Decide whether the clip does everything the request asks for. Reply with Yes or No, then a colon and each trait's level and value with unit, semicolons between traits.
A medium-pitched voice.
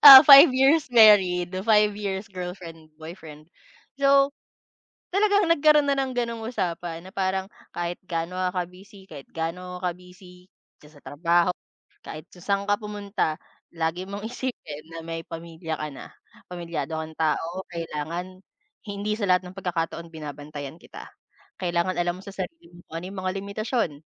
Yes: medium, 180 Hz